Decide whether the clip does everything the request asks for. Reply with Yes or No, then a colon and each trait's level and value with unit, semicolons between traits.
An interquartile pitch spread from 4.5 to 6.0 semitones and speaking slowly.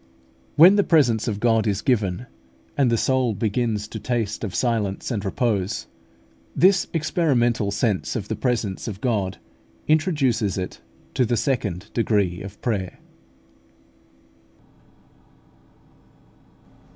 No: average, 4.0 semitones; slow, 115 wpm